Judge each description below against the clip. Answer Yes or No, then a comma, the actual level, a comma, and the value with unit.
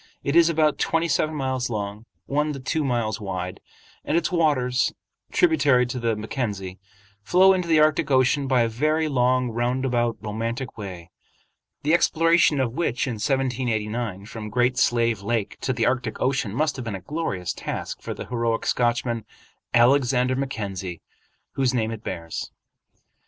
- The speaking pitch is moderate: No, low, 125 Hz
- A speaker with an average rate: Yes, average, 155 wpm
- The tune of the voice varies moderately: Yes, average, 4.0 semitones